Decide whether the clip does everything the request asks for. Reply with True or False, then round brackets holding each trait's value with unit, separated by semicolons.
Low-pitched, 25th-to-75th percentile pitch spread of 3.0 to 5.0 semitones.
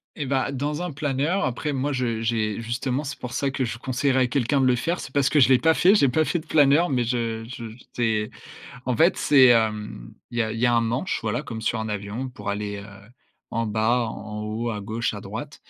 True (120 Hz; 3.8 semitones)